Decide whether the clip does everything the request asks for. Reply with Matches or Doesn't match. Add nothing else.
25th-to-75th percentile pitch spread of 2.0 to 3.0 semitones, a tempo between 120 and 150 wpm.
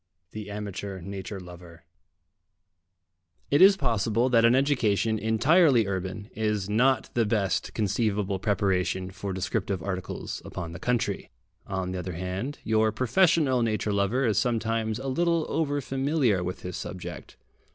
Doesn't match